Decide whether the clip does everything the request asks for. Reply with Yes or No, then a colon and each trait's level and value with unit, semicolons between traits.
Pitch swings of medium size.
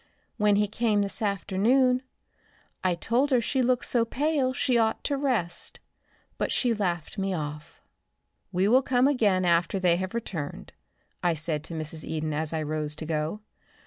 No: wide, 6.8 semitones